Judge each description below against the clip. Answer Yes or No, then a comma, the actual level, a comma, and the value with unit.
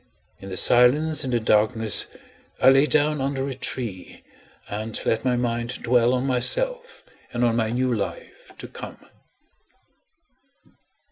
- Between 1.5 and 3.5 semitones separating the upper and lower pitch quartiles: Yes, average, 3.0 semitones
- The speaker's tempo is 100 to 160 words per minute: Yes, average, 140 wpm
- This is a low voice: Yes, low, 125 Hz